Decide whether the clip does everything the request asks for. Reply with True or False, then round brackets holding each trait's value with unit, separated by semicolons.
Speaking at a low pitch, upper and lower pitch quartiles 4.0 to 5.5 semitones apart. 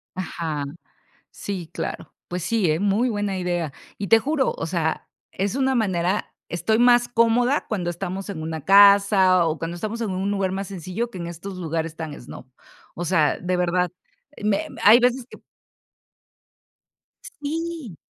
False (190 Hz; 4.6 semitones)